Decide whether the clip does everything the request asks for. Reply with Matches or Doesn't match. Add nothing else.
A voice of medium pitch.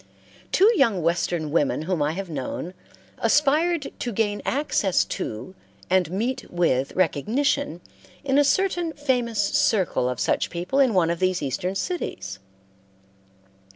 Doesn't match